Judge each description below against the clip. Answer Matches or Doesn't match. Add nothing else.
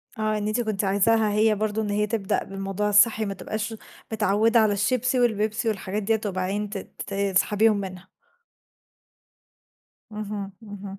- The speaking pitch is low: Doesn't match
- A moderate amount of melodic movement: Doesn't match